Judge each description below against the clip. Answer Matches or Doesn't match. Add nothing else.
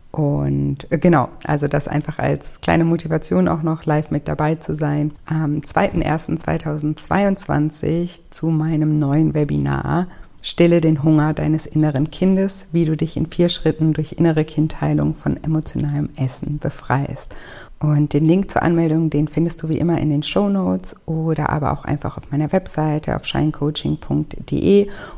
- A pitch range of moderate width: Doesn't match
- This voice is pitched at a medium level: Matches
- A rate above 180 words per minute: Doesn't match